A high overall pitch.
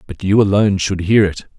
No: low, 100 Hz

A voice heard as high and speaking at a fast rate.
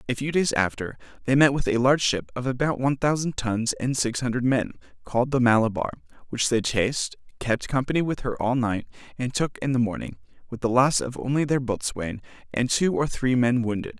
No: low, 125 Hz; fast, 210 wpm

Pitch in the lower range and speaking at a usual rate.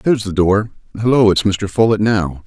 Yes: low, 105 Hz; average, 195 wpm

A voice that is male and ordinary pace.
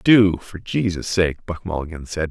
Yes: male; average, 180 wpm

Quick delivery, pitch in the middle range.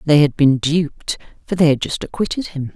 Yes: fast, 220 wpm; medium, 155 Hz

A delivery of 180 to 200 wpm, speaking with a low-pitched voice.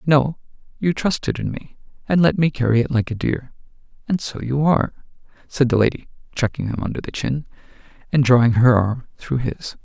Yes: average, 190 wpm; low, 130 Hz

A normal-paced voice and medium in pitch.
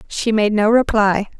No: average, 170 wpm; high, 215 Hz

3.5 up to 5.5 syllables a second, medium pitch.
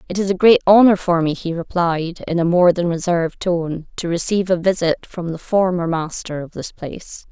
Yes: 5.2 syllables/s; medium, 175 Hz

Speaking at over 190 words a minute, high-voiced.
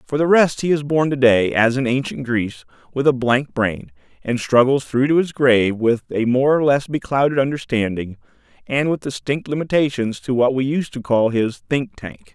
No: average, 200 wpm; low, 130 Hz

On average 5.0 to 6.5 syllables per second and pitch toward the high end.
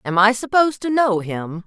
Yes: 5.1 syllables/s; high, 215 Hz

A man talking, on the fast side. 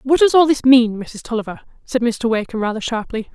No: female; fast, 215 wpm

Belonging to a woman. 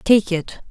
Yes: female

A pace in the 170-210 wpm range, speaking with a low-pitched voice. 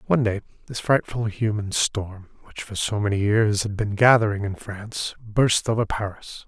Yes: average, 175 wpm; low, 110 Hz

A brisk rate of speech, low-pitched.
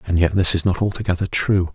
Yes: fast, 240 wpm; very low, 90 Hz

